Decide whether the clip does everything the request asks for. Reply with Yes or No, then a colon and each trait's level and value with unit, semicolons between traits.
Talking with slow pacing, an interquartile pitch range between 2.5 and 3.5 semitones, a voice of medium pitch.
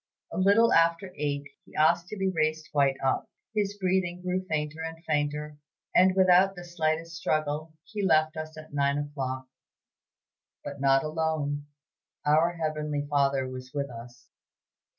No: average, 150 wpm; average, 3.2 semitones; medium, 155 Hz